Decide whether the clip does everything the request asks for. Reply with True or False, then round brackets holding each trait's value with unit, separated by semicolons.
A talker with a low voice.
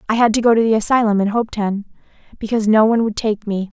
False (215 Hz)